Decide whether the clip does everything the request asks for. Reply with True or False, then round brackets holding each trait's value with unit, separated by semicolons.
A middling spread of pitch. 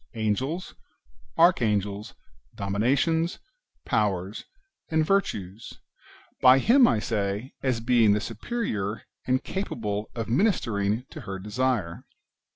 True (4.8 semitones)